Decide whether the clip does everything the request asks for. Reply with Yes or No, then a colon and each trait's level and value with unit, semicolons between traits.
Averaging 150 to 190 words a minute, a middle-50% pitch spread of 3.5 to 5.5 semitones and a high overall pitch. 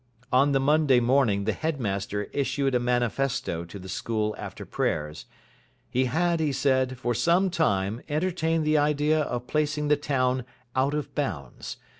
No: average, 155 wpm; average, 4.1 semitones; low, 135 Hz